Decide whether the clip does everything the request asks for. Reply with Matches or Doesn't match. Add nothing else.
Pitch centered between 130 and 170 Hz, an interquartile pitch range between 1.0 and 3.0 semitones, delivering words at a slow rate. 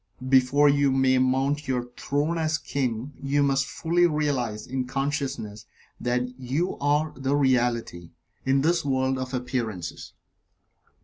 Matches